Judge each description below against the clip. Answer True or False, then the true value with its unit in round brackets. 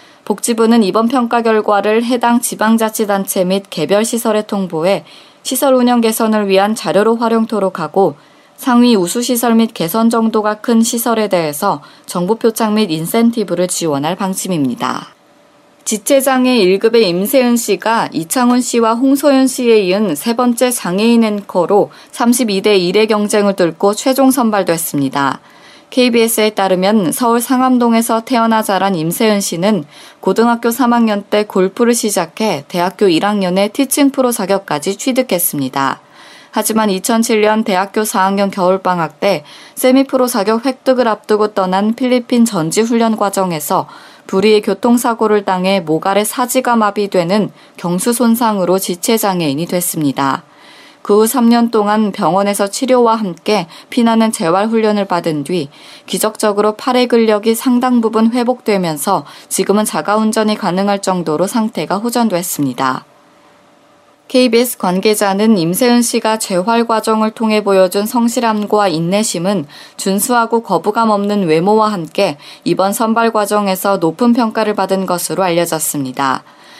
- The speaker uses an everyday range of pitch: True (3.6 semitones)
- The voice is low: False (215 Hz)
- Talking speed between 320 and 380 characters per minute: False (310 characters per minute)